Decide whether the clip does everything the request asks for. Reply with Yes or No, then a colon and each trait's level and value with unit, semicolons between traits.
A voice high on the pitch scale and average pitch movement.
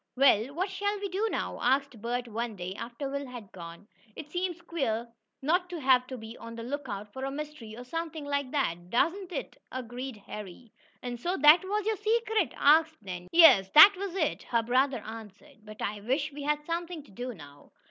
No: very high, 270 Hz; wide, 6.4 semitones